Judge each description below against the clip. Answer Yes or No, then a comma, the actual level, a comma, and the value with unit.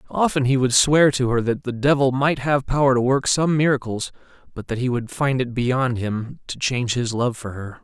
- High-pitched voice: No, low, 130 Hz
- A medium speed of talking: No, fast, 230 wpm